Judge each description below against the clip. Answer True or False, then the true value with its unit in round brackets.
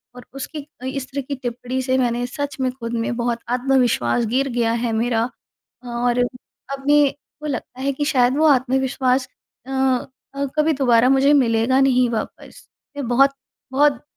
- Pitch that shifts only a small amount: True (2.1 semitones)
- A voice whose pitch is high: True (260 Hz)